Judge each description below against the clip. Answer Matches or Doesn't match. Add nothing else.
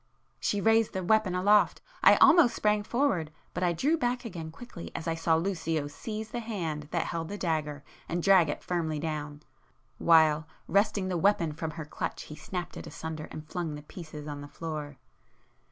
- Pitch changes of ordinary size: Matches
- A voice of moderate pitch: Matches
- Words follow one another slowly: Doesn't match